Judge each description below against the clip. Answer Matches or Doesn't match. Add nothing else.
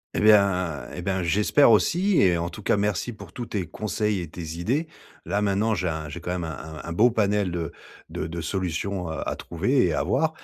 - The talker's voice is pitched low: Matches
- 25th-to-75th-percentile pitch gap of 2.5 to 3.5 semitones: Doesn't match